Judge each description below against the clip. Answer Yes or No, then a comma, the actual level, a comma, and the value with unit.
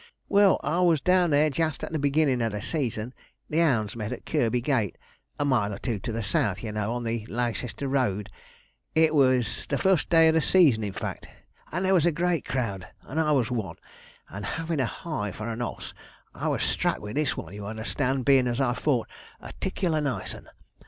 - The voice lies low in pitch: Yes, low, 130 Hz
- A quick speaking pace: Yes, fast, 215 wpm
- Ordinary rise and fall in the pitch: No, wide, 5.9 semitones